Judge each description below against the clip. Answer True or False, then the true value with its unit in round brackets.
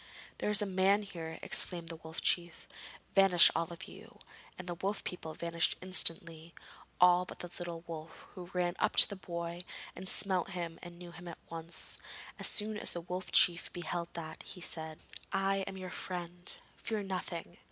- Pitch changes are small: True (1.9 semitones)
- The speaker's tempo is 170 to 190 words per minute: True (185 wpm)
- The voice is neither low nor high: True (175 Hz)